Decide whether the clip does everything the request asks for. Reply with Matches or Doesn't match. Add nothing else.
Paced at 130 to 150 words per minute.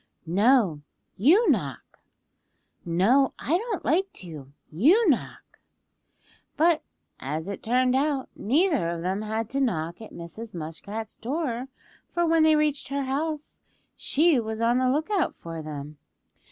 Matches